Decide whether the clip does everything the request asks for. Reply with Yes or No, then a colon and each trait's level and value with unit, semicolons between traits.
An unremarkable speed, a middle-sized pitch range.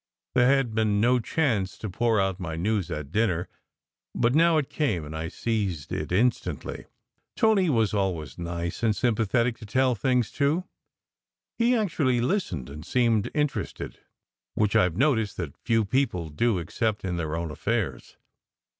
No: average, 160 wpm; wide, 6.1 semitones